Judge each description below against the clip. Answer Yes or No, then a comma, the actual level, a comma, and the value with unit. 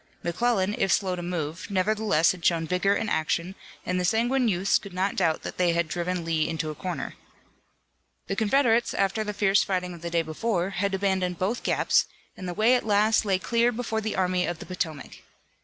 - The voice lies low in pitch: No, medium, 185 Hz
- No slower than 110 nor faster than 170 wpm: No, fast, 205 wpm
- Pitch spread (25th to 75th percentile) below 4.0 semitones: Yes, average, 3.6 semitones